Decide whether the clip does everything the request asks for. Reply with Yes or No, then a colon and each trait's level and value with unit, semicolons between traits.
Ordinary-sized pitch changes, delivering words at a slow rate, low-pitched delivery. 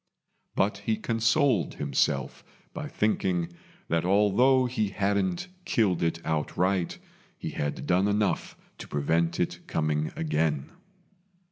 Yes: average, 4.4 semitones; slow, 115 wpm; very low, 95 Hz